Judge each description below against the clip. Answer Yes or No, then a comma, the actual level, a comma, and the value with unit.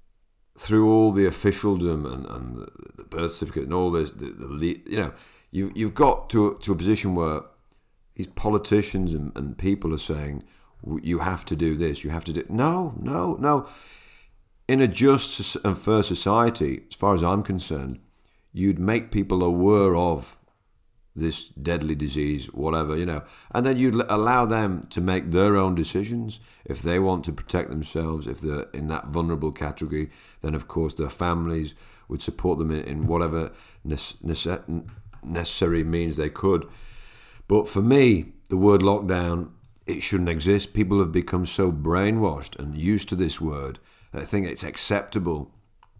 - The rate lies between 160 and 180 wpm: Yes, average, 170 wpm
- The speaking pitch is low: Yes, very low, 90 Hz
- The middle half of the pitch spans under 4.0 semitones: No, average, 4.4 semitones